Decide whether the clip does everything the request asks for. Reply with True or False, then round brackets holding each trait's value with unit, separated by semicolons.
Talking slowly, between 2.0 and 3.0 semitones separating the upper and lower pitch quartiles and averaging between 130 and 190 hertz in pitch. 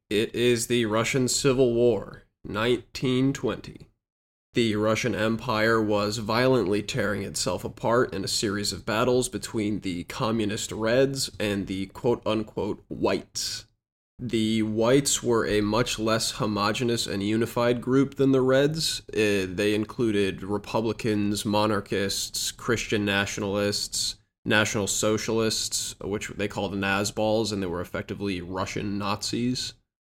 False (120 wpm; 2.7 semitones; 110 Hz)